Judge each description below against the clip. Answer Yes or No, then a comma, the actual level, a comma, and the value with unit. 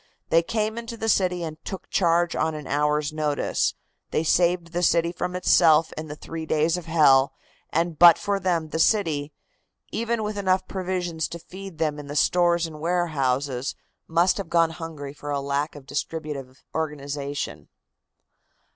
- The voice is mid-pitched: Yes, medium, 165 Hz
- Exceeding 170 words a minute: No, average, 165 wpm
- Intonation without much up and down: No, average, 3.1 semitones